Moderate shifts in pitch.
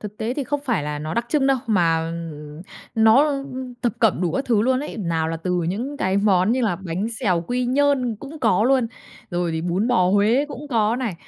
No: wide, 6.4 semitones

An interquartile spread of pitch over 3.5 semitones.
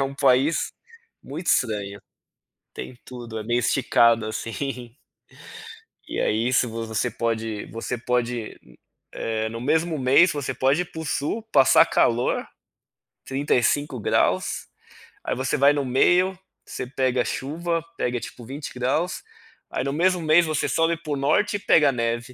Yes: average, 4.3 semitones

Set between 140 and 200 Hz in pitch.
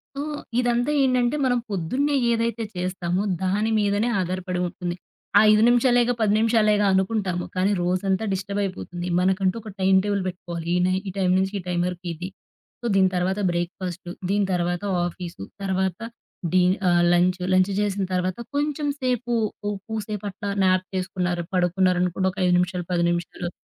Yes: high, 190 Hz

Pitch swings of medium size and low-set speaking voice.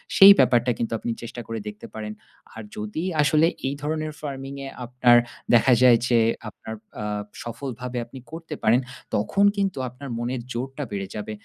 Yes: average, 3.4 semitones; low, 125 Hz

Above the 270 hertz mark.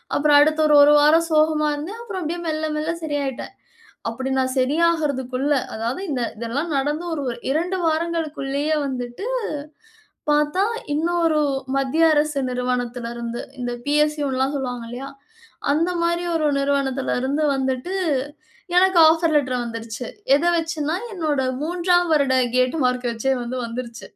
Yes: very high, 290 Hz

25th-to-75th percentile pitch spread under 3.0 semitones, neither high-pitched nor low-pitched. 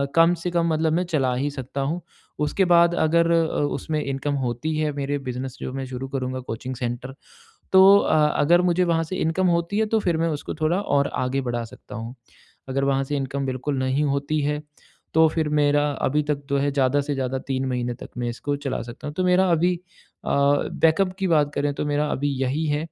No: average, 3.7 semitones; medium, 145 Hz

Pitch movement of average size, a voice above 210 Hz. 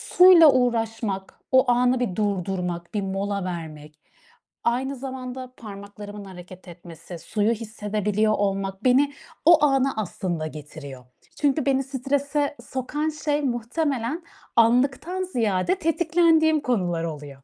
No: wide, 6.3 semitones; high, 230 Hz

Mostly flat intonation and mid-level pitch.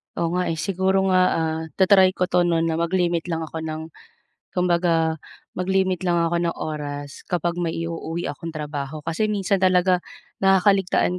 Yes: narrow, 2.3 semitones; medium, 175 Hz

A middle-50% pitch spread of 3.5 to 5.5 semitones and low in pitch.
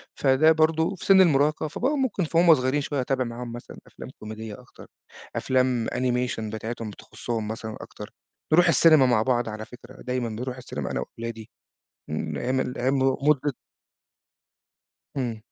Yes: average, 4.5 semitones; low, 125 Hz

